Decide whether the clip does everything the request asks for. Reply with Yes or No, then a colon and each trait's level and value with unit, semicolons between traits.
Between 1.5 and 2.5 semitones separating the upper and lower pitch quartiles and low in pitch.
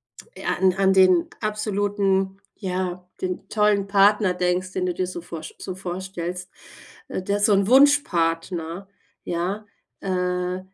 No: narrow, 1.9 semitones; medium, 185 Hz